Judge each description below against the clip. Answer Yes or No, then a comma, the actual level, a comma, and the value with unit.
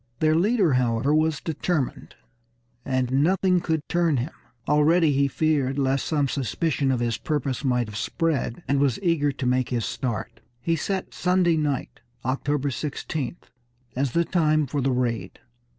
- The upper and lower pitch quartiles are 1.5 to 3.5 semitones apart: No, average, 3.9 semitones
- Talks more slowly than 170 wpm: Yes, average, 155 wpm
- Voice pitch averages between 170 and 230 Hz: No, medium, 145 Hz